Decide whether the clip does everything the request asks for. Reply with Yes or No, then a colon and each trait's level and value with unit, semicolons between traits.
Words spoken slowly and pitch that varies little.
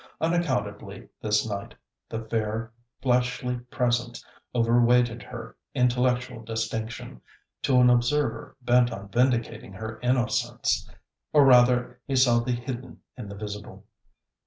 Yes: slow, 120 wpm; narrow, 2.0 semitones